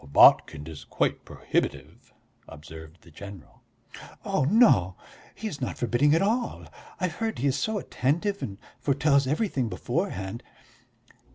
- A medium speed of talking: No, slow, 130 wpm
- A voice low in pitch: Yes, low, 130 Hz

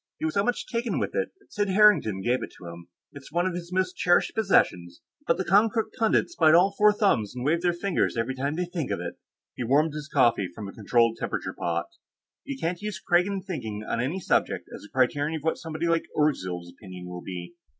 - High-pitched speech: No, medium, 155 Hz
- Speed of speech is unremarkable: No, fast, 225 wpm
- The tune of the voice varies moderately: No, wide, 8.5 semitones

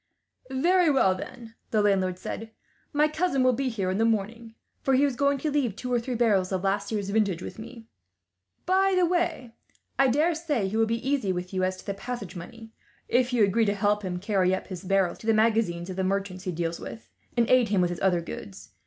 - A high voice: Yes, high, 220 Hz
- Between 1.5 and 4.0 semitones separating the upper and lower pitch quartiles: No, average, 5.2 semitones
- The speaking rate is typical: No, fast, 230 wpm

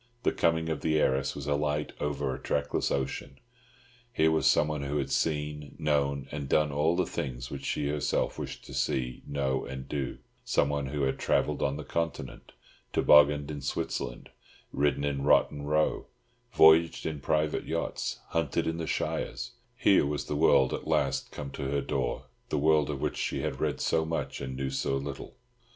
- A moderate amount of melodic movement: No, narrow, 2.1 semitones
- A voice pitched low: Yes, very low, 70 Hz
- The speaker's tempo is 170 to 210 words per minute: Yes, average, 180 wpm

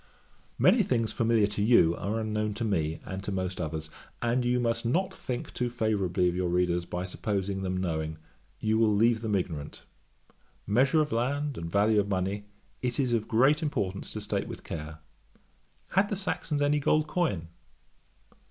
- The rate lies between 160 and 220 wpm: Yes, average, 175 wpm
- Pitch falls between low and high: No, low, 105 Hz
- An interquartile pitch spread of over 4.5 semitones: Yes, average, 4.9 semitones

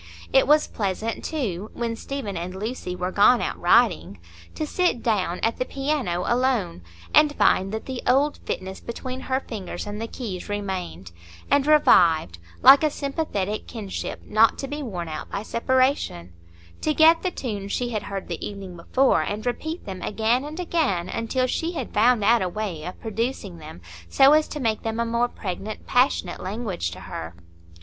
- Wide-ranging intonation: Yes, wide, 5.8 semitones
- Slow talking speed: No, average, 180 wpm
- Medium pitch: No, high, 225 Hz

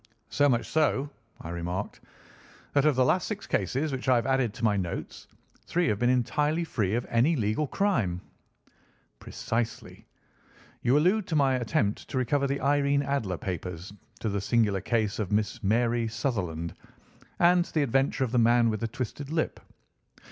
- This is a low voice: Yes, low, 120 Hz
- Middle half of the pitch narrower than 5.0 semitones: No, average, 5.3 semitones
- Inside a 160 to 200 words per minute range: Yes, average, 170 wpm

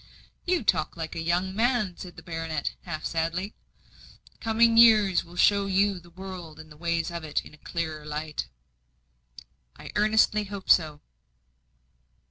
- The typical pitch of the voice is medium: Yes, medium, 175 Hz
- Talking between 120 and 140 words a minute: No, average, 150 wpm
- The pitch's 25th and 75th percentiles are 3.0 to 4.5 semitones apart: Yes, average, 4.0 semitones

